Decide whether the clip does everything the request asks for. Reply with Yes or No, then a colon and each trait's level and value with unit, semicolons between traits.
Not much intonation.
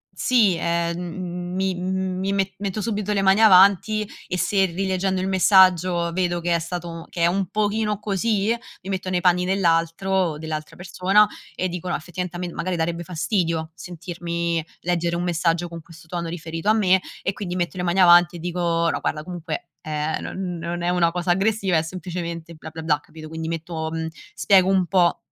Yes: narrow, 2.1 semitones